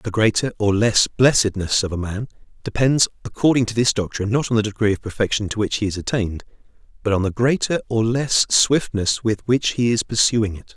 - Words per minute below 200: No, fast, 205 wpm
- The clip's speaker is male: Yes, male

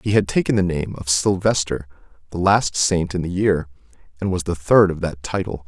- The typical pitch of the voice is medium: No, very low, 90 Hz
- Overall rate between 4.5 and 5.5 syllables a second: Yes, 5.1 syllables/s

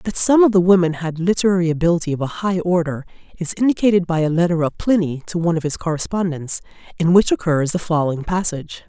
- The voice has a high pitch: No, medium, 170 Hz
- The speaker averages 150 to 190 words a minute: No, fast, 205 wpm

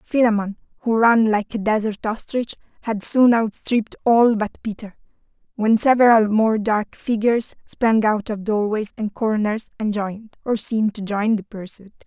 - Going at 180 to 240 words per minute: No, average, 160 wpm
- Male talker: No, female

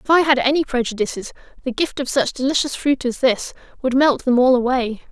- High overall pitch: Yes, very high, 260 Hz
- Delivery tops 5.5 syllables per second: Yes, 5.8 syllables/s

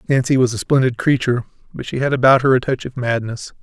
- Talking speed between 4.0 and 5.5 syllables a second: No, 6.5 syllables/s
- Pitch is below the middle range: Yes, low, 125 Hz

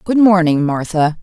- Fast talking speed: No, average, 145 wpm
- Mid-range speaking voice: Yes, medium, 175 Hz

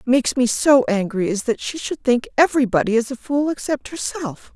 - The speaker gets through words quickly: Yes, fast, 210 wpm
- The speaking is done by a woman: Yes, female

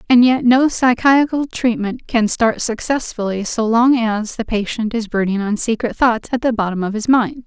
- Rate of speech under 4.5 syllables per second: No, 4.7 syllables/s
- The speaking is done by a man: No, female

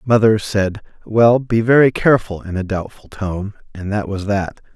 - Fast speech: No, average, 175 wpm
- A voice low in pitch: Yes, low, 105 Hz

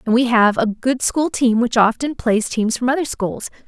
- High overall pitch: Yes, high, 240 Hz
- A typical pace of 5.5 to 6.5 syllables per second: No, 4.8 syllables/s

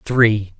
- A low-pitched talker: Yes, low, 105 Hz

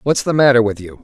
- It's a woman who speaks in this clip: No, male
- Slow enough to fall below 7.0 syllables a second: Yes, 6.5 syllables/s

